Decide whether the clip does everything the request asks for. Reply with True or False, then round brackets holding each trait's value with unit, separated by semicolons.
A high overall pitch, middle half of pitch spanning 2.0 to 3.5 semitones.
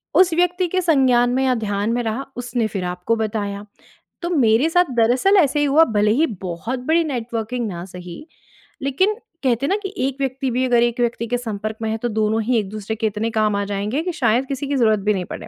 False (235 Hz; 4.3 semitones)